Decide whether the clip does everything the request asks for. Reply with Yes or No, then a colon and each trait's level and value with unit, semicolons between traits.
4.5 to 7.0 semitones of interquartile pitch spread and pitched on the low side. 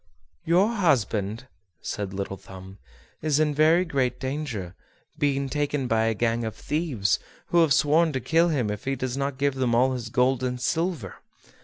Yes: average, 5.1 semitones; low, 130 Hz